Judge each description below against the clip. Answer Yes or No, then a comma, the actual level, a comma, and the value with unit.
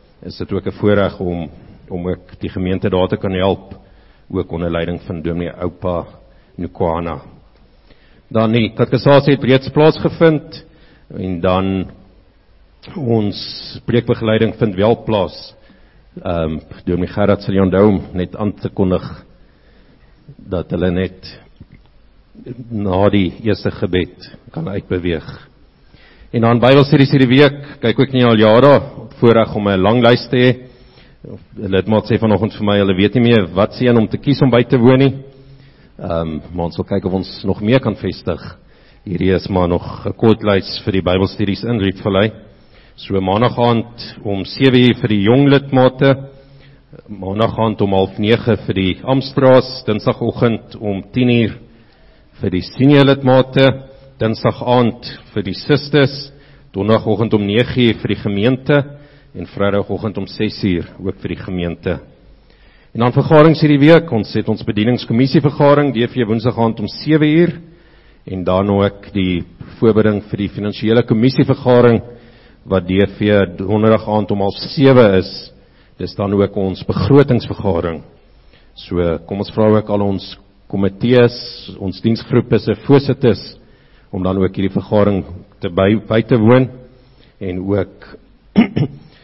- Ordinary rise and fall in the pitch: Yes, average, 4.7 semitones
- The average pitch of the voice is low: Yes, low, 110 Hz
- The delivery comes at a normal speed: Yes, average, 145 wpm